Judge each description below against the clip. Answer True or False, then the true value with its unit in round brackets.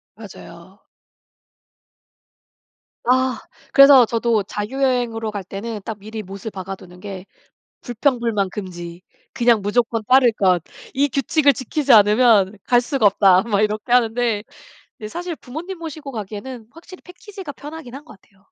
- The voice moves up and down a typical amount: True (4.7 semitones)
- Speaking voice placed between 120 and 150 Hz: False (230 Hz)